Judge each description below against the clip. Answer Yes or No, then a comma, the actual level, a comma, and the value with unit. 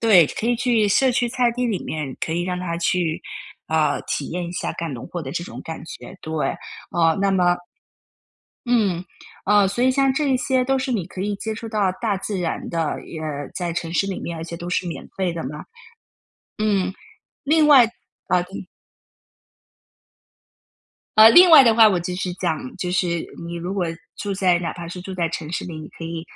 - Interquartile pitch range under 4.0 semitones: No, average, 4.7 semitones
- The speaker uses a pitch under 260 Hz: Yes, medium, 185 Hz